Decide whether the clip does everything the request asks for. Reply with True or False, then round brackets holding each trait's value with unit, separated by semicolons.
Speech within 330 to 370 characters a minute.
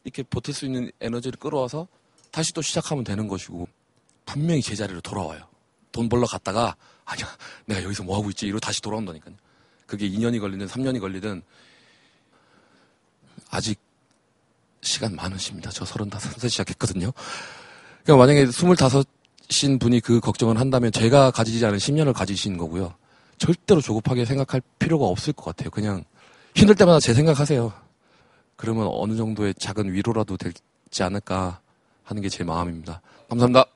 True (345 characters per minute)